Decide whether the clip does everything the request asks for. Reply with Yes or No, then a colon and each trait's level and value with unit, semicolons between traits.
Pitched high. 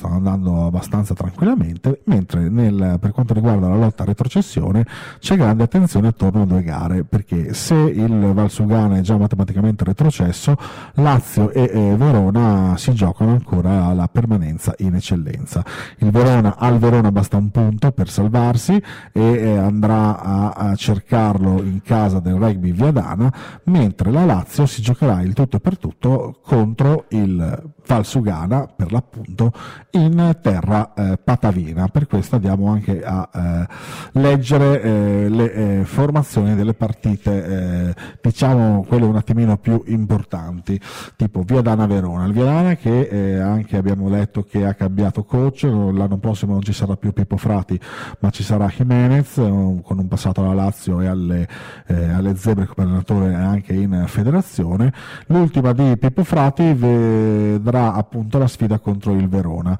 No: low, 105 Hz